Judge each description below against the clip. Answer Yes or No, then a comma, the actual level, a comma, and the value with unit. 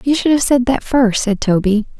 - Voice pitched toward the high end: Yes, high, 240 Hz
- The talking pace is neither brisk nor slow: No, fast, 240 wpm